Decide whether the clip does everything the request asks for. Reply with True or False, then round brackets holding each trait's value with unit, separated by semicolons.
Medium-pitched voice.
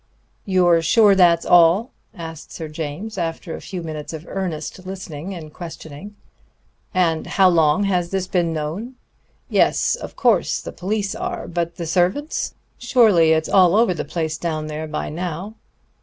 True (175 Hz)